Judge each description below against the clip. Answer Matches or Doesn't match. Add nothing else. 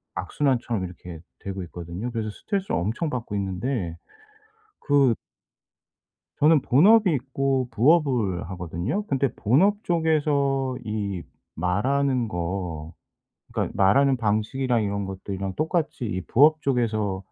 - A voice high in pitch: Doesn't match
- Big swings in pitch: Matches